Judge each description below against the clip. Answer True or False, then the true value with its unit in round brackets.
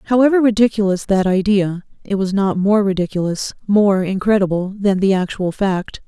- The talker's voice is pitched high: True (195 Hz)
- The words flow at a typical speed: True (150 wpm)